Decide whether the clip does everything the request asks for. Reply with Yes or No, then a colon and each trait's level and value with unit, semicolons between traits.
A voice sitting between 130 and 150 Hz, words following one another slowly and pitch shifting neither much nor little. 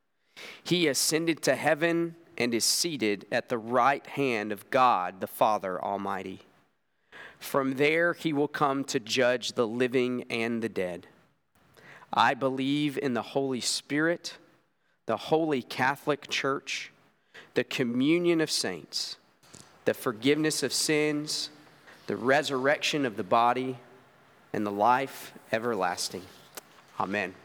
Yes: medium, 140 Hz; slow, 120 wpm; average, 4.2 semitones